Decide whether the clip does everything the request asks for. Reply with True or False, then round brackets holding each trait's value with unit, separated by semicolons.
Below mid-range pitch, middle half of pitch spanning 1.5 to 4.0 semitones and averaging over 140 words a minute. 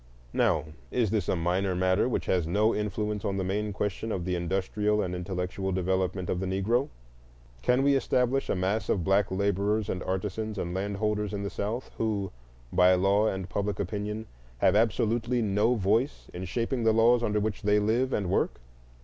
True (100 Hz; 2.8 semitones; 185 wpm)